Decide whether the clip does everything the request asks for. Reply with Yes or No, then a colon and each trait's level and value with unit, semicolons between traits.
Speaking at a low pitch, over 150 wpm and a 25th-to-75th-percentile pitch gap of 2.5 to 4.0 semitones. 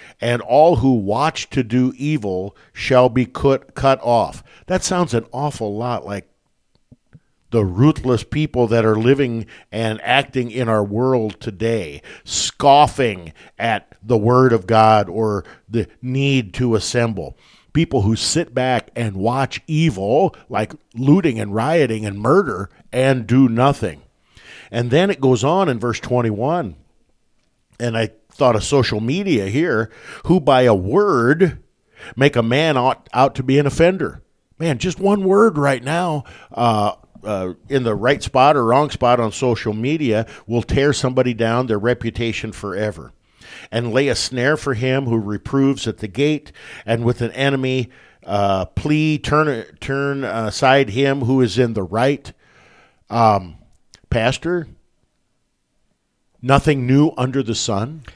No: low, 125 Hz; average, 145 wpm; average, 3.7 semitones